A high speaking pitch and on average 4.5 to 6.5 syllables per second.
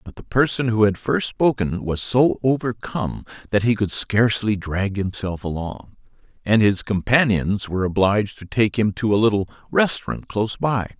No: low, 105 Hz; 5.0 syllables/s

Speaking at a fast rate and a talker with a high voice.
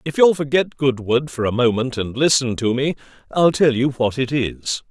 No: fast, 210 wpm; low, 130 Hz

